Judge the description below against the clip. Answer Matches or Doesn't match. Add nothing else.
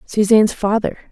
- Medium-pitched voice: Doesn't match